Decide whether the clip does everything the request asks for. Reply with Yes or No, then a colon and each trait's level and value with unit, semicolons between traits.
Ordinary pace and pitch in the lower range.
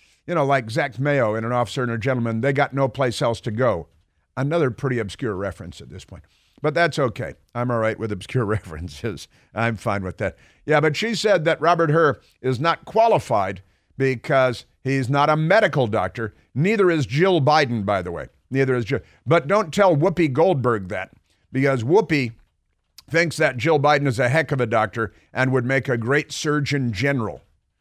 Yes: average, 190 wpm; low, 130 Hz